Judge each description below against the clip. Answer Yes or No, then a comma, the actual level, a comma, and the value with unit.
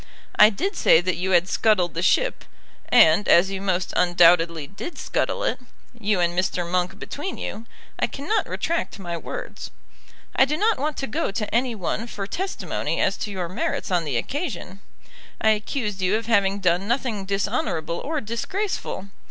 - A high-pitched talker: Yes, high, 200 Hz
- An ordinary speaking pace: Yes, average, 175 wpm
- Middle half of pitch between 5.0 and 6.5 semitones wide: Yes, average, 5.3 semitones